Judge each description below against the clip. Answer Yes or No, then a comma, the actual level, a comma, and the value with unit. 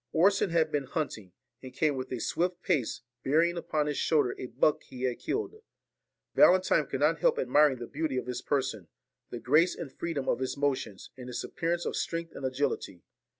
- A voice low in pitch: No, medium, 145 Hz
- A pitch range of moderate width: Yes, average, 4.4 semitones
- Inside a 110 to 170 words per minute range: No, average, 195 wpm